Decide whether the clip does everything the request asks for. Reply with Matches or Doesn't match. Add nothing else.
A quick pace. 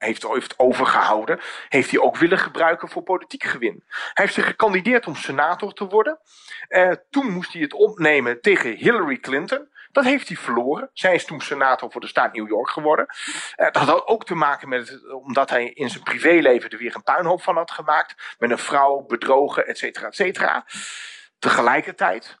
Doesn't match